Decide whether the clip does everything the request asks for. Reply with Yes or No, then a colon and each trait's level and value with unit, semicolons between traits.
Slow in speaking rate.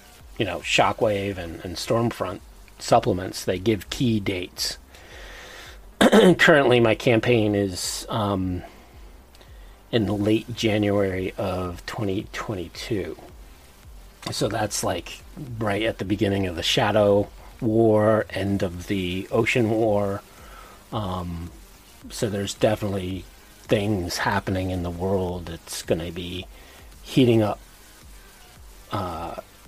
Yes: slow, 105 wpm